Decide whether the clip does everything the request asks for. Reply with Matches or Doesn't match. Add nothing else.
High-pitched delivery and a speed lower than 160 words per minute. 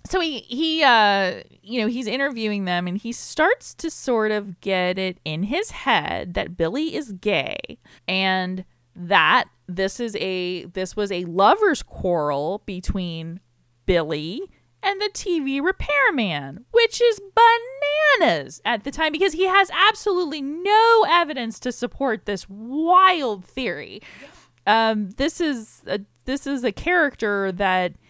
Matches